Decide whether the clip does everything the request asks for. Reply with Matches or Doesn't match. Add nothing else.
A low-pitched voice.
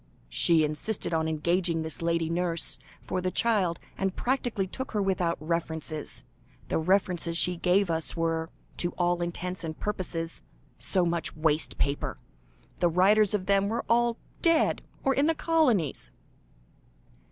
Doesn't match